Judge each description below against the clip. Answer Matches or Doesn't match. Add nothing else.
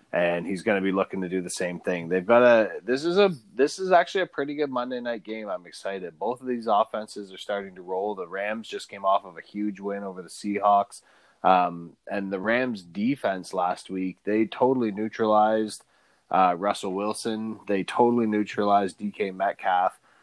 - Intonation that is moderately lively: Matches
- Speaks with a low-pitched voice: Matches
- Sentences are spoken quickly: Doesn't match